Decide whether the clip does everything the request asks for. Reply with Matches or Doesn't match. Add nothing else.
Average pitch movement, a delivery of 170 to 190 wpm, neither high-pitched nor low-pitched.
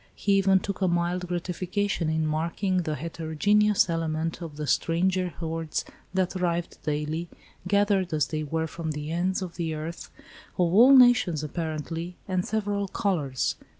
Doesn't match